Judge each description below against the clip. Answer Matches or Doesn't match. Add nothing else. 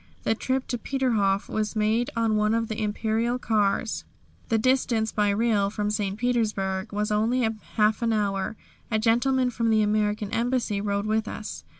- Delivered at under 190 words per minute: Matches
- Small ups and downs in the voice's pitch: Matches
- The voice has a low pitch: Doesn't match